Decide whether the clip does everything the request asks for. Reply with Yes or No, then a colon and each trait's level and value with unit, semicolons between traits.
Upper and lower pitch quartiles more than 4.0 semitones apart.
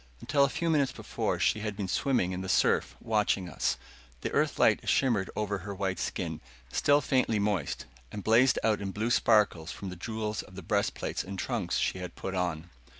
No: average, 3.4 semitones